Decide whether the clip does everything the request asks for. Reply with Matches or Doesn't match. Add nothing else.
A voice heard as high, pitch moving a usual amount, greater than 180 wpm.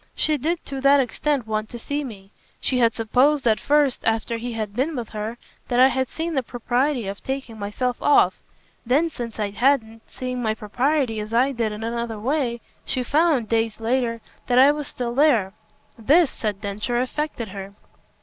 Matches